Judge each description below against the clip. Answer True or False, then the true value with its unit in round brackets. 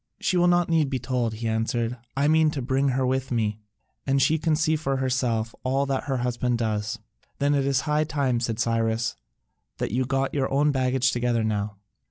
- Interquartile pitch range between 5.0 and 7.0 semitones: False (3.2 semitones)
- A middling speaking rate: False (210 wpm)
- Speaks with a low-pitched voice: True (130 Hz)